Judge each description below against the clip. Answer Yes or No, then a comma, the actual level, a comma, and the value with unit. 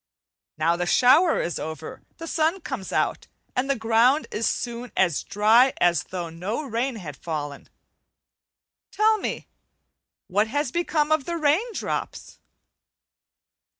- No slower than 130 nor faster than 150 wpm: Yes, slow, 135 wpm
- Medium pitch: No, high, 240 Hz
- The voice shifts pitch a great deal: Yes, wide, 9.0 semitones